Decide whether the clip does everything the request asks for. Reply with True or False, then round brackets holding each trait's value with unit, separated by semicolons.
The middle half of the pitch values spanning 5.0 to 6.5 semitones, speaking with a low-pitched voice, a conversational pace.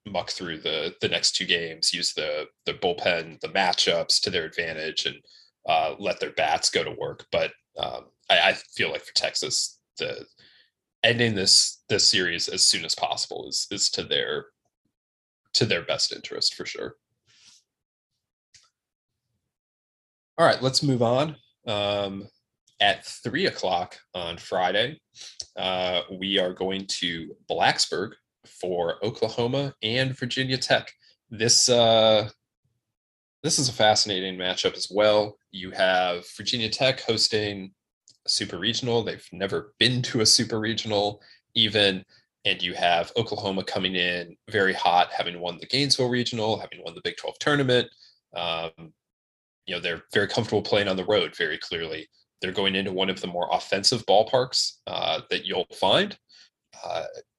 True (5.3 semitones; 110 Hz; 150 wpm)